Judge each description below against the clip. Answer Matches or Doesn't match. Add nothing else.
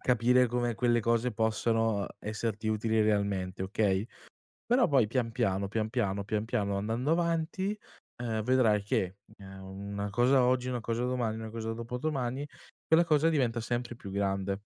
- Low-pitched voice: Matches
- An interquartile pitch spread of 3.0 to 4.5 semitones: Matches